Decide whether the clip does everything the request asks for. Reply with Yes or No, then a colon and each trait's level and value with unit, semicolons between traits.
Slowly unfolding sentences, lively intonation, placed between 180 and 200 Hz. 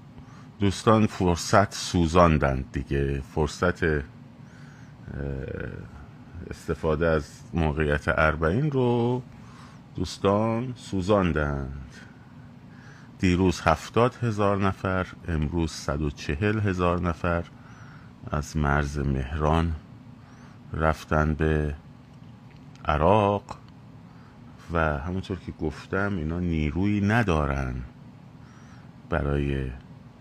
No: slow, 70 wpm; wide, 6.8 semitones; very low, 85 Hz